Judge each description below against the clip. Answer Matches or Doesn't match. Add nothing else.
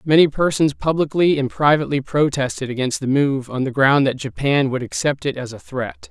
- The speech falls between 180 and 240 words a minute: Matches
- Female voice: Doesn't match